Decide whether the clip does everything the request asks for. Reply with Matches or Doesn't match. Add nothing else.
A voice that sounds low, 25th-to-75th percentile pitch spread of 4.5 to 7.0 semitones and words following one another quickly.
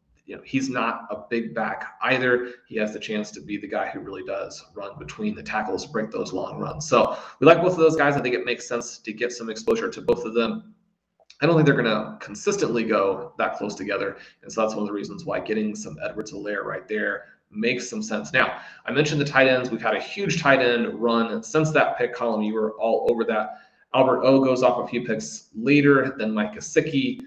Matches